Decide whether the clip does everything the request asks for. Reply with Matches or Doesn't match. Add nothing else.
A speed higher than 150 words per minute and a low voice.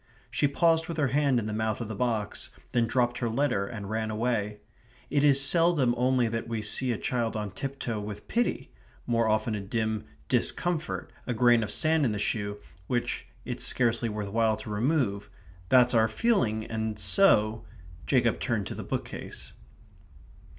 Matches